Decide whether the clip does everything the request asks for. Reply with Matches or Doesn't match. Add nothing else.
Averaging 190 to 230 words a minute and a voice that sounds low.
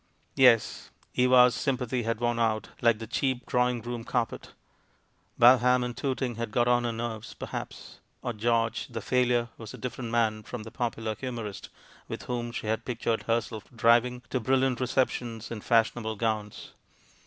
Doesn't match